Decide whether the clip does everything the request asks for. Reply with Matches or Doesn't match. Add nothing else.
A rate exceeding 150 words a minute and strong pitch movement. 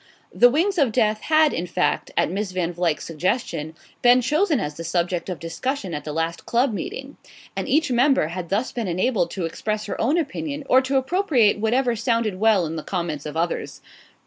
Matches